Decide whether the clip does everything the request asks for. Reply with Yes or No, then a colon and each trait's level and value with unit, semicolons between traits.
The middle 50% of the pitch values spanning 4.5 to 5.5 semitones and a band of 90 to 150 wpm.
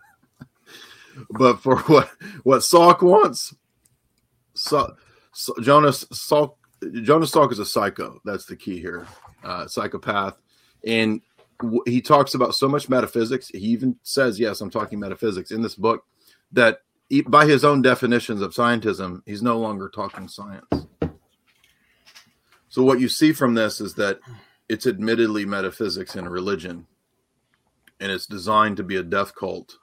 No: average, 4.0 semitones; average, 145 wpm